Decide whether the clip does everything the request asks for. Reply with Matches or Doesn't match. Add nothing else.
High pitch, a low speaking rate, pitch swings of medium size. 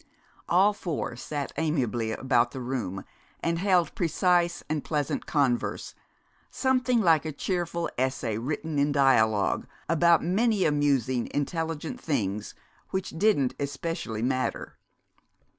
Doesn't match